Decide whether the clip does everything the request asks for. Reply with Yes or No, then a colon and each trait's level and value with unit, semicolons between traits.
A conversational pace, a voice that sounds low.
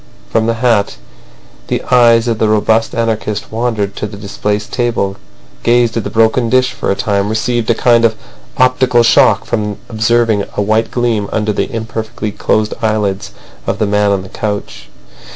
Yes: average, 170 wpm; low, 110 Hz